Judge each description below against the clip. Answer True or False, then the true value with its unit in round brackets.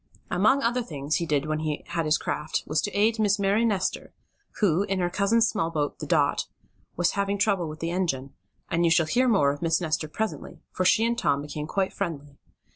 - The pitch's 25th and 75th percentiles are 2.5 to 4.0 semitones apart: False (5.0 semitones)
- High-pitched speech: False (175 Hz)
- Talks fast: True (220 wpm)